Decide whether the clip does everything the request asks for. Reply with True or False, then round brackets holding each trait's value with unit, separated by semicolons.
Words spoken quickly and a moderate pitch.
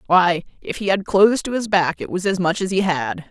True (270 wpm; 180 Hz)